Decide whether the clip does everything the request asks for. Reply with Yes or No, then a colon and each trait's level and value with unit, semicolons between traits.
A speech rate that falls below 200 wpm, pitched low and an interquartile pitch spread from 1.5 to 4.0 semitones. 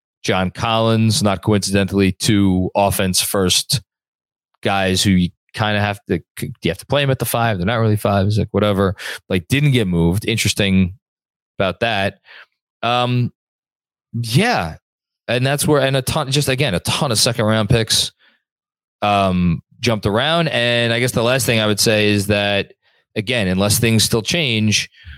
Yes: average, 165 wpm; low, 110 Hz; average, 3.5 semitones